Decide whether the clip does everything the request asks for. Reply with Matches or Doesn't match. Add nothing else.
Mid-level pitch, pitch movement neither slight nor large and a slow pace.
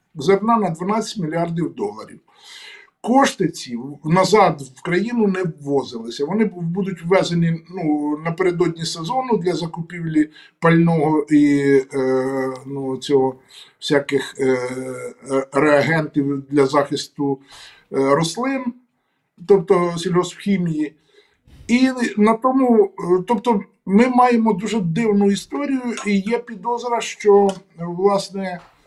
Doesn't match